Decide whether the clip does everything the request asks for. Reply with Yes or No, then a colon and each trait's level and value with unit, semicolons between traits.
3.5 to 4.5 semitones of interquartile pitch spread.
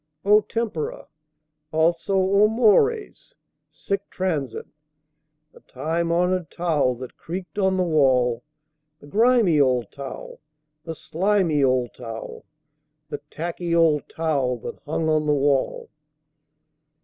No: average, 5.1 semitones